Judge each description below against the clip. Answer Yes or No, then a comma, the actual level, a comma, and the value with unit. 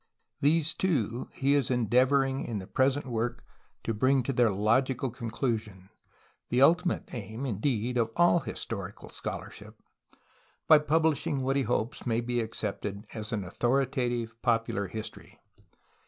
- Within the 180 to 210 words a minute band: No, average, 145 wpm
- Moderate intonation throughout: Yes, average, 3.5 semitones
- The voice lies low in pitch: Yes, low, 120 Hz